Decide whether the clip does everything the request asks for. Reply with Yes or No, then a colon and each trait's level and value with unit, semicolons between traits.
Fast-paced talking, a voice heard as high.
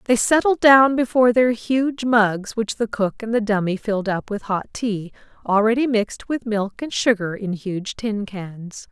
No: average, 190 wpm; high, 220 Hz